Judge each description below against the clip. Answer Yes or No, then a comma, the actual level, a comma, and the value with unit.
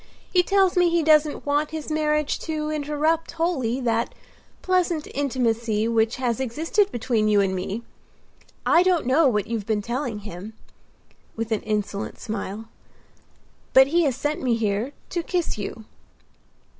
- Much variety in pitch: Yes, wide, 6.0 semitones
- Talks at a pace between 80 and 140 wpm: No, average, 150 wpm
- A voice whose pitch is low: No, very high, 260 Hz